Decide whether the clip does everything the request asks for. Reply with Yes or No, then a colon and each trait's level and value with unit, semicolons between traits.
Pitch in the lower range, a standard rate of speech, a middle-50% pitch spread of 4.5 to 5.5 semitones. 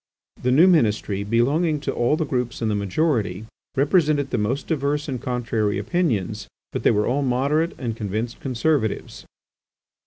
Yes: low, 125 Hz; average, 155 wpm; average, 5.2 semitones